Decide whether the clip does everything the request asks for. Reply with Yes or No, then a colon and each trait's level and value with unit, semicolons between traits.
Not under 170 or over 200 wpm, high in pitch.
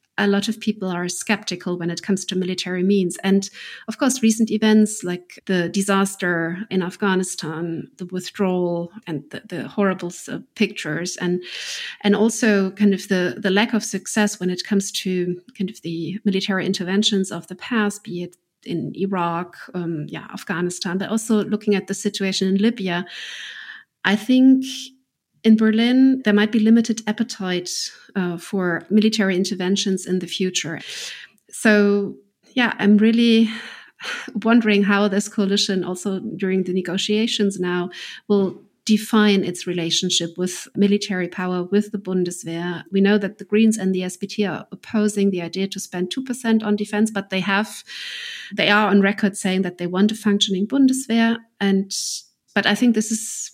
No: average, 160 wpm; high, 195 Hz